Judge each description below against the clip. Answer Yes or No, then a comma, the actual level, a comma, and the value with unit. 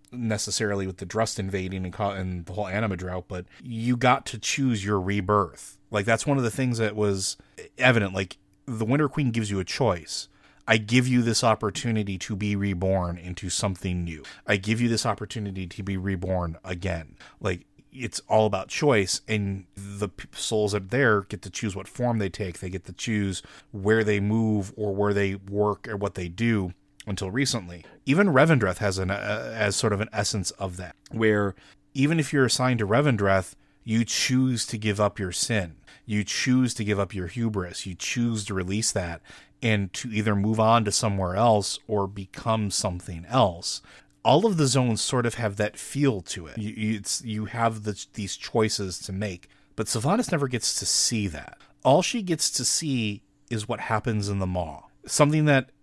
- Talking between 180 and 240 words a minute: Yes, average, 195 wpm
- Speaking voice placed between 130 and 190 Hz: No, low, 105 Hz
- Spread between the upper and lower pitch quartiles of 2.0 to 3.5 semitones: Yes, average, 3.1 semitones